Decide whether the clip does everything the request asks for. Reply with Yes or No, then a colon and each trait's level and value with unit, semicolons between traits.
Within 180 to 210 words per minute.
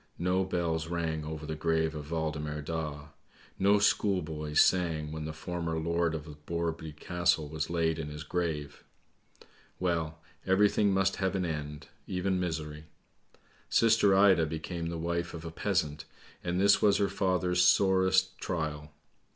No: average, 145 wpm